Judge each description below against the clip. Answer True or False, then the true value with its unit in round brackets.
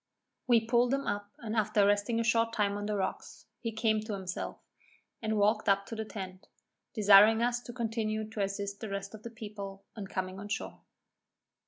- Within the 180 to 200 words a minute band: True (195 wpm)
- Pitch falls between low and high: False (215 Hz)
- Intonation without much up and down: True (2.1 semitones)